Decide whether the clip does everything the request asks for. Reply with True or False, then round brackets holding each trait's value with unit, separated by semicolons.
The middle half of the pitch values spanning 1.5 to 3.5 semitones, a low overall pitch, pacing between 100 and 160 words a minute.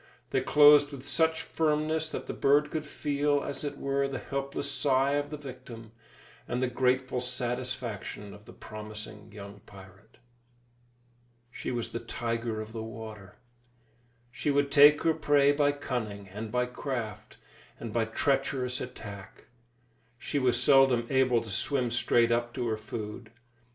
False (4.0 semitones; 125 Hz; 150 wpm)